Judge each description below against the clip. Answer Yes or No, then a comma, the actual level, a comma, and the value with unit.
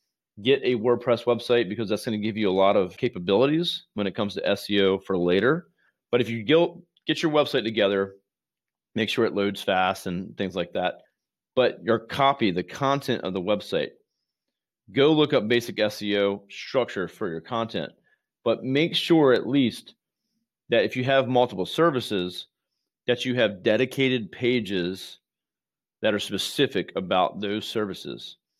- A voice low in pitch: Yes, low, 115 Hz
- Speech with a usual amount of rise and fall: Yes, average, 5.0 semitones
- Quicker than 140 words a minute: Yes, average, 160 wpm